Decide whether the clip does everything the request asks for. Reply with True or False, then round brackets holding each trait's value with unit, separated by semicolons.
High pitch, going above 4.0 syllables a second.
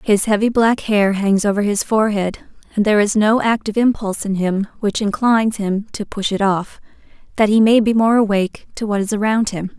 True (210 Hz; 5.5 syllables/s)